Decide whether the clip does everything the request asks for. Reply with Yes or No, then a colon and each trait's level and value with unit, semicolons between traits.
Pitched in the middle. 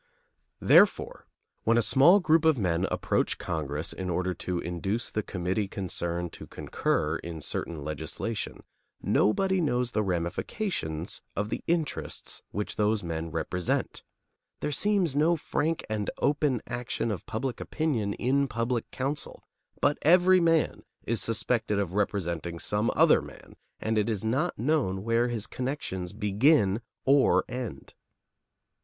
No: low, 110 Hz